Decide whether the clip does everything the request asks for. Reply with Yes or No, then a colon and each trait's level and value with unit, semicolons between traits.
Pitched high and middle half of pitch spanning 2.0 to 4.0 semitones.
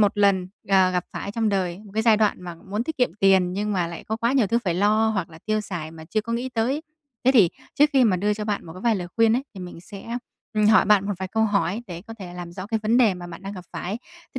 Yes: high, 205 Hz; average, 3.4 semitones